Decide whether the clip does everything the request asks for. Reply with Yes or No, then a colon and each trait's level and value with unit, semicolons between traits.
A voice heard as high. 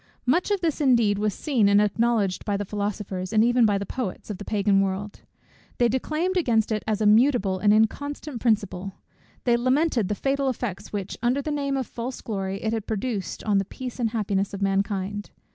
Yes: high, 215 Hz